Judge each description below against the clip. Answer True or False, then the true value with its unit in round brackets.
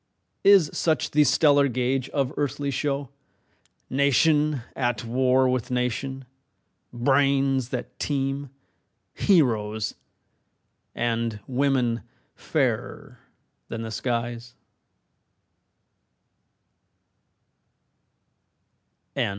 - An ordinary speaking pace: False (70 wpm)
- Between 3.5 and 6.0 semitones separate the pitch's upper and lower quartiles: False (2.8 semitones)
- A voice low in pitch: True (130 Hz)